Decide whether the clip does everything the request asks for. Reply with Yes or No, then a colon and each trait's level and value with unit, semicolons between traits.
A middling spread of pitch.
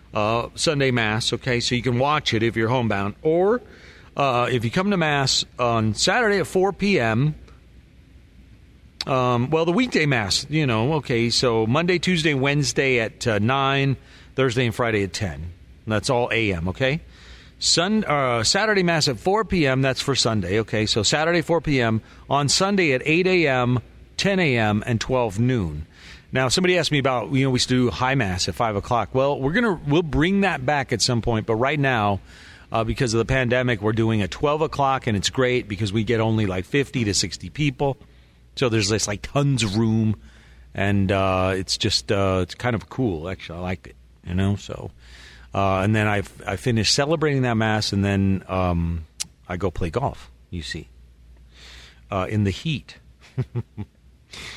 No: wide, 5.7 semitones